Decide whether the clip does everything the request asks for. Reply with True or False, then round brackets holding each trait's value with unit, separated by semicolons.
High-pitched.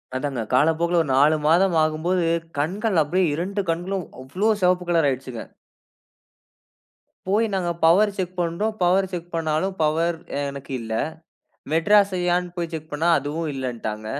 False (170 Hz)